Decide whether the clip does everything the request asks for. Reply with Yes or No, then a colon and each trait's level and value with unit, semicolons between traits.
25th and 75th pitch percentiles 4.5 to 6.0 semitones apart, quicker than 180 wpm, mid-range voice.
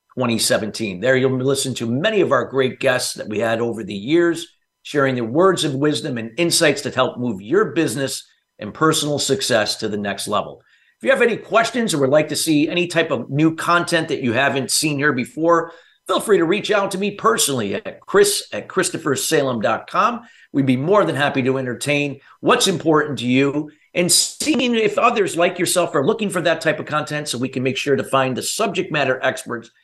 Yes: average, 4.8 semitones; fast, 205 wpm; medium, 150 Hz